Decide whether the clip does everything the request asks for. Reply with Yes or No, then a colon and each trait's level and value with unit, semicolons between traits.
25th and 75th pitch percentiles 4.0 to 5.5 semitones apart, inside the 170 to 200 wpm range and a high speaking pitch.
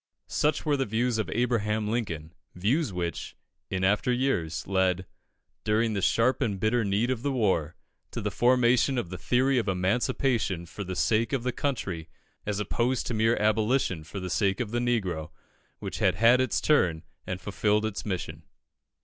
No: average, 4.8 semitones; average, 175 wpm; low, 110 Hz